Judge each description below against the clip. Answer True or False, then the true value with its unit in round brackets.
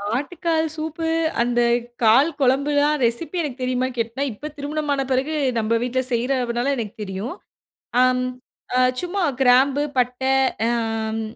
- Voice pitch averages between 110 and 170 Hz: False (255 Hz)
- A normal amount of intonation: True (3.6 semitones)